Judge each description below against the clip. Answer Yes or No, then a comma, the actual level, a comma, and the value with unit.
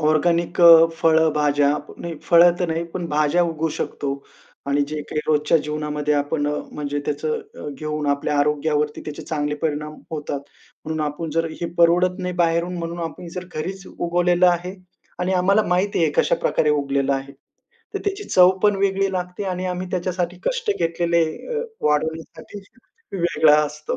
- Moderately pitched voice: Yes, medium, 160 Hz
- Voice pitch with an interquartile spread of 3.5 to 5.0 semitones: No, average, 3.0 semitones